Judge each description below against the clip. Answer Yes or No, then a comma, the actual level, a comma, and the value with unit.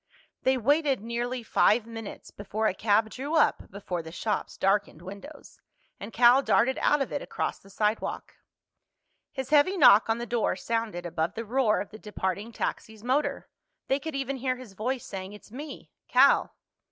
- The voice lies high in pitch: Yes, high, 230 Hz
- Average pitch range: Yes, average, 4.3 semitones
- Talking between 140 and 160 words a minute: No, average, 170 wpm